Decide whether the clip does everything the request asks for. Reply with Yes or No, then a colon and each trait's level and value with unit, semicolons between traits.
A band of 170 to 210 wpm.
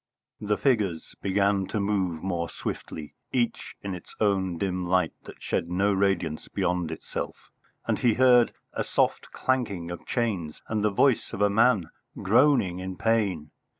No: average, 155 wpm